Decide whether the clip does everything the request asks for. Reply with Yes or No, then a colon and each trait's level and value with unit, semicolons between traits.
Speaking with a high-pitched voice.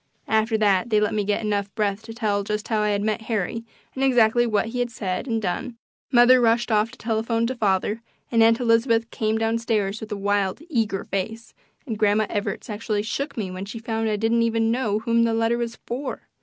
Yes: high, 225 Hz